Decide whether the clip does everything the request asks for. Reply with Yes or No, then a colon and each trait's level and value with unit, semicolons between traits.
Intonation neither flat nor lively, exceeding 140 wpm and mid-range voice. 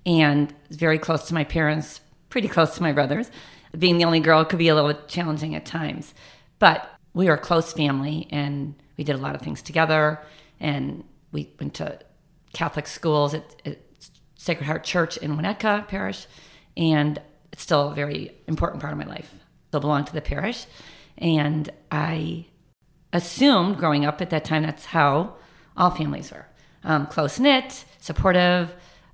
No: narrow, 2.1 semitones; average, 170 wpm; medium, 155 Hz